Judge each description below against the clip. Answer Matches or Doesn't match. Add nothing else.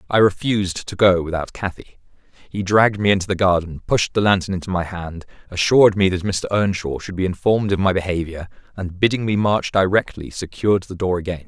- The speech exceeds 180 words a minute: Matches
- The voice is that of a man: Matches